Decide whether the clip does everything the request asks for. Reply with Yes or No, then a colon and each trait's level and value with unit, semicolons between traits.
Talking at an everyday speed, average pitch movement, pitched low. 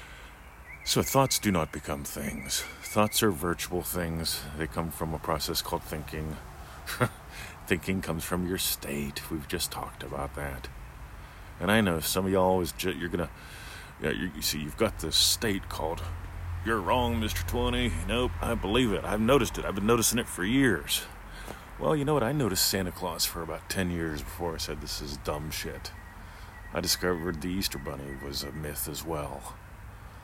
Yes: average, 185 wpm; average, 4.1 semitones; very low, 85 Hz